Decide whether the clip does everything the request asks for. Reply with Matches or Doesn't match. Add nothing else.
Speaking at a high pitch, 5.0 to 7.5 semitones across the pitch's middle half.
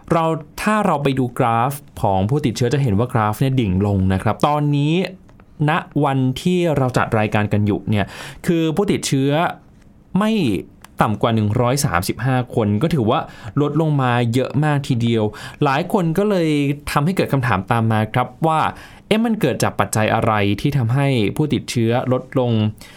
Doesn't match